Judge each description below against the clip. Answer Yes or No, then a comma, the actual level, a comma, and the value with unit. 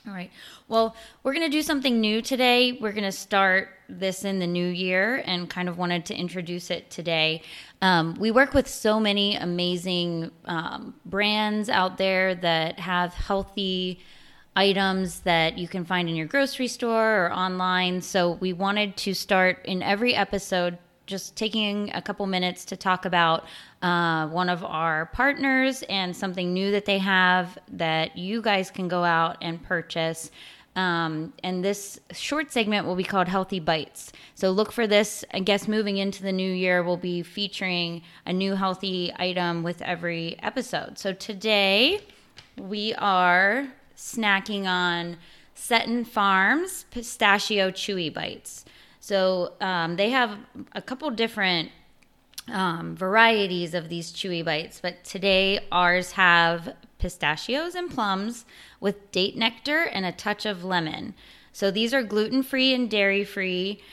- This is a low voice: No, high, 190 Hz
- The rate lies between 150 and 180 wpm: Yes, average, 155 wpm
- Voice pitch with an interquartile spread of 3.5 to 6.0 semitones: No, average, 3.1 semitones